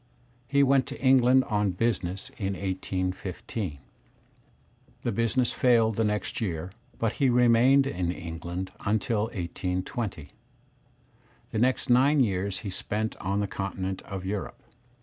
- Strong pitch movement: No, average, 4.5 semitones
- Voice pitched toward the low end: Yes, low, 105 Hz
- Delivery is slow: Yes, slow, 130 wpm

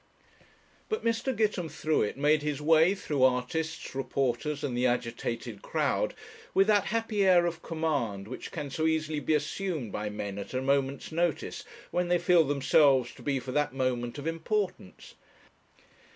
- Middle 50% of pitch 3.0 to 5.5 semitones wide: Yes, average, 4.8 semitones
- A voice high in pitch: No, medium, 150 Hz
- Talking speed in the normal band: Yes, average, 155 wpm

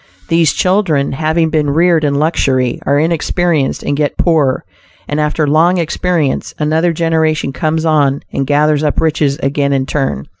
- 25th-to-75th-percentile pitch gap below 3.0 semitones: Yes, narrow, 2.4 semitones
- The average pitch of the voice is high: No, medium, 155 Hz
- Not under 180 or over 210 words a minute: No, average, 155 wpm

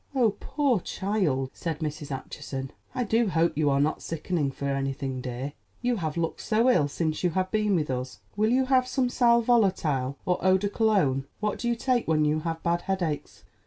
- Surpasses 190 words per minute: Yes, average, 200 wpm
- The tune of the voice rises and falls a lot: Yes, wide, 7.3 semitones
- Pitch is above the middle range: No, medium, 170 Hz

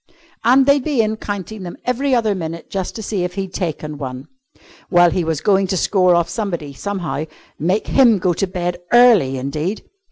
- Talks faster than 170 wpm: Yes, average, 190 wpm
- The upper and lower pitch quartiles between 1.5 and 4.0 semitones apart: No, average, 4.5 semitones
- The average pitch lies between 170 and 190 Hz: Yes, medium, 185 Hz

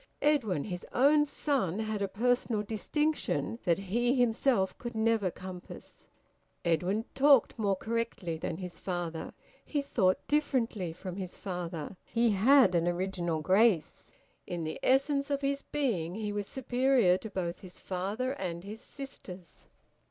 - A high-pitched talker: Yes, high, 205 Hz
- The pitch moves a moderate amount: No, wide, 5.9 semitones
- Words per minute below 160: Yes, average, 145 wpm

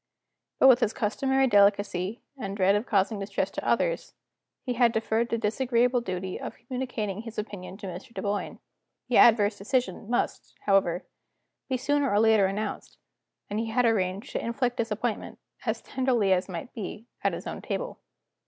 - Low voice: No, high, 220 Hz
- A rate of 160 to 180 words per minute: Yes, average, 165 wpm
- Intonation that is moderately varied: Yes, average, 3.5 semitones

